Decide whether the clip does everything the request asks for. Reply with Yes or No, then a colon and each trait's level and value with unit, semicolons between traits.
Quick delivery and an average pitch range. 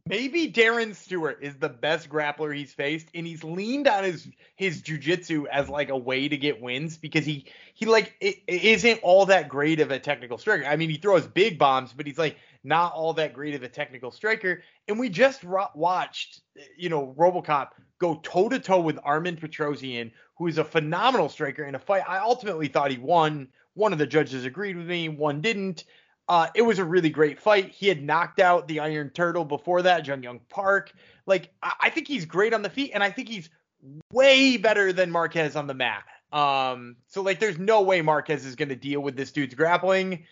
Yes: fast, 215 wpm; average, 4.8 semitones